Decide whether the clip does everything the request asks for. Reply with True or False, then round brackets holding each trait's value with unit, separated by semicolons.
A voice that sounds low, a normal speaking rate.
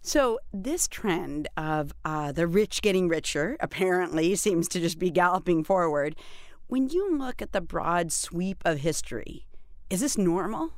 False (180 Hz; 155 wpm)